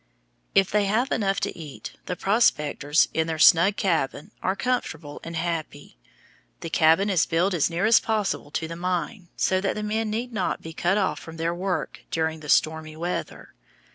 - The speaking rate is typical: Yes, average, 185 wpm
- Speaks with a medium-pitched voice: Yes, medium, 175 Hz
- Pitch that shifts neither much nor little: Yes, average, 3.9 semitones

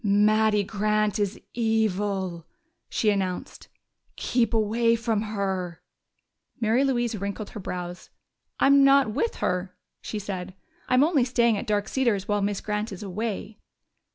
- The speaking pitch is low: No, high, 210 Hz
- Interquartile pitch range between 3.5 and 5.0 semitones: No, average, 2.7 semitones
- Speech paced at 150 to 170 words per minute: No, slow, 135 wpm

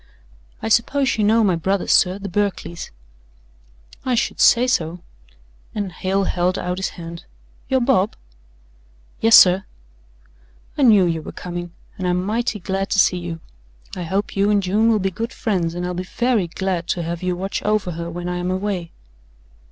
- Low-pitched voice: No, high, 190 Hz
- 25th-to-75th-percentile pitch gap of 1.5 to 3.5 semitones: Yes, average, 3.1 semitones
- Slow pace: No, average, 175 wpm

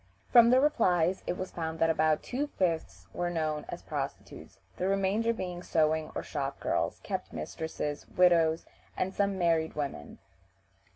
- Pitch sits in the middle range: Yes, medium, 170 Hz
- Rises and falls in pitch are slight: No, average, 3.3 semitones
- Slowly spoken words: No, average, 155 wpm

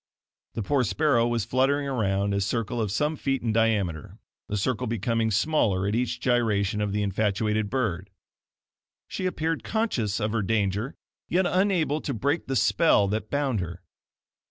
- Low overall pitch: Yes, low, 115 Hz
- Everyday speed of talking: Yes, average, 165 wpm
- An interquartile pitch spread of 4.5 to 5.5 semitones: Yes, average, 5.0 semitones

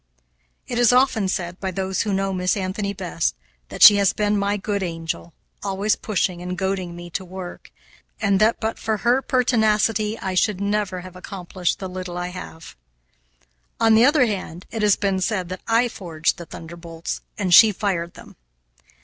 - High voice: Yes, high, 195 Hz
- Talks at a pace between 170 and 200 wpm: Yes, average, 180 wpm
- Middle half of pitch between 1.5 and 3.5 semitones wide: Yes, average, 2.9 semitones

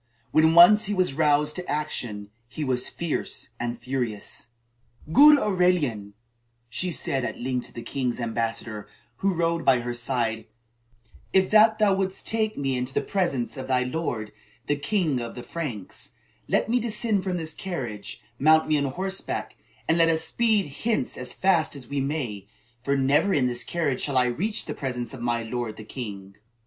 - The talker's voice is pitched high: No, medium, 140 Hz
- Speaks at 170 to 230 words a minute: Yes, average, 180 wpm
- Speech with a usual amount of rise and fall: No, wide, 6.7 semitones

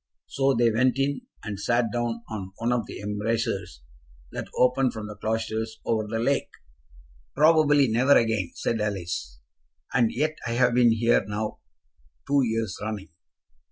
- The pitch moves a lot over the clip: No, average, 2.8 semitones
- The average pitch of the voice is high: No, low, 115 Hz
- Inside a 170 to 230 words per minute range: No, average, 155 wpm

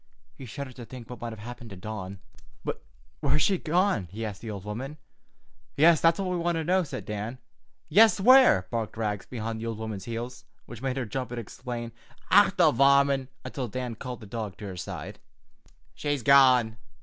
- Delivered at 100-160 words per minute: No, average, 200 wpm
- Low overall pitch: Yes, low, 120 Hz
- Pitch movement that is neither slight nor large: Yes, average, 4.1 semitones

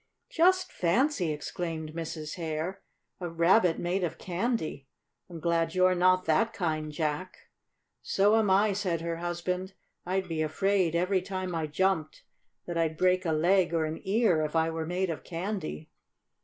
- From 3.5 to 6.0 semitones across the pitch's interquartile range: No, average, 2.8 semitones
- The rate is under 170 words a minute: Yes, average, 160 wpm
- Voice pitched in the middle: Yes, medium, 175 Hz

